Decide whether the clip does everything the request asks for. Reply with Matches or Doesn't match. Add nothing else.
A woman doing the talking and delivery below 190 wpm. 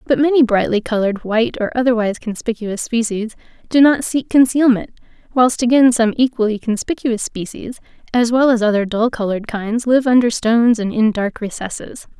Matches